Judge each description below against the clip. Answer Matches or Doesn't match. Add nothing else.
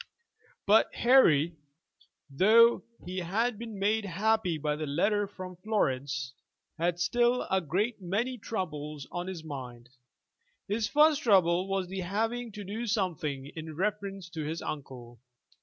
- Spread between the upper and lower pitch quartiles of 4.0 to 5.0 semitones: Doesn't match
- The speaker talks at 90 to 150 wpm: Matches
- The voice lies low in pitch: Doesn't match